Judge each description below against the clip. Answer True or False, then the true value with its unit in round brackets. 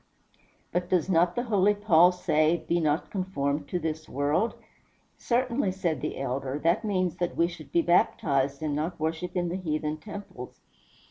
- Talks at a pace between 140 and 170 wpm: True (165 wpm)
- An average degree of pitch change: True (3.3 semitones)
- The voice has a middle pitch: True (170 Hz)